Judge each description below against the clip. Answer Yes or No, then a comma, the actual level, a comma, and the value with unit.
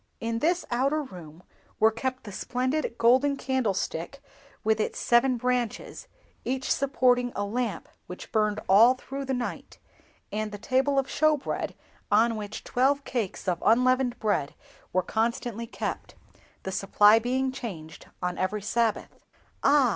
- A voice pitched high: Yes, high, 235 Hz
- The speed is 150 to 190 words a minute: No, average, 140 wpm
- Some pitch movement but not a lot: Yes, average, 3.8 semitones